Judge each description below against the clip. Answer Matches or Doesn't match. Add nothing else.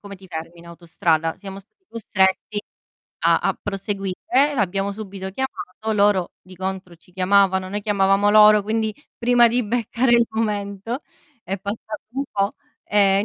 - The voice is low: Doesn't match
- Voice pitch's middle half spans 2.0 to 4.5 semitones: Matches